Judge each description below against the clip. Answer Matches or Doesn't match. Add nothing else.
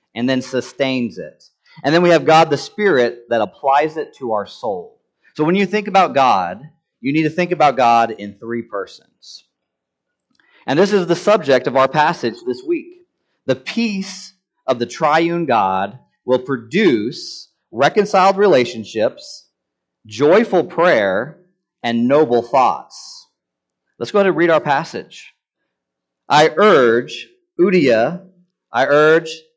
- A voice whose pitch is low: Doesn't match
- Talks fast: Doesn't match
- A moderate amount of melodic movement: Doesn't match